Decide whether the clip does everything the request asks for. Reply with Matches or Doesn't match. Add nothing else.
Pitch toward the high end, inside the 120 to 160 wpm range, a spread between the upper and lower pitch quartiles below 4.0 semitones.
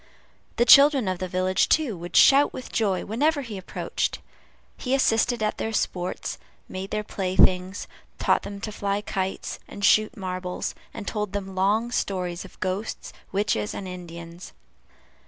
Matches